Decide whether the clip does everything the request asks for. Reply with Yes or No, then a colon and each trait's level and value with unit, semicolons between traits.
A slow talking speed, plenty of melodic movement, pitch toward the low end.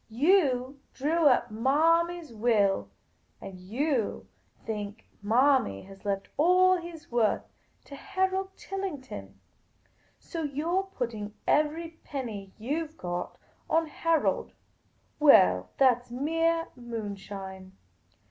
No: slow, 110 wpm; wide, 7.9 semitones; very high, 265 Hz